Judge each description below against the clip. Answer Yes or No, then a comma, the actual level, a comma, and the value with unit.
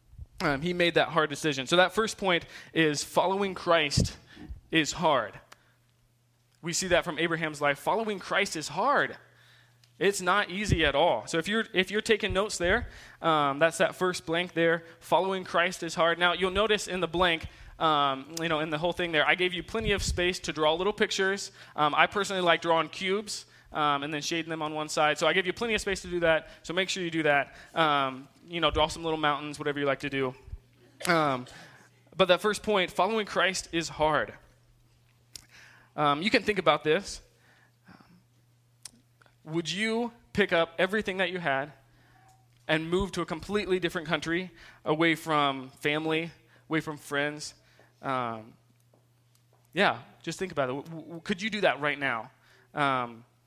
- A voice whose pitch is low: No, medium, 160 Hz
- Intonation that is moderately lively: Yes, average, 4.6 semitones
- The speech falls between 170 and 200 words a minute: Yes, average, 185 wpm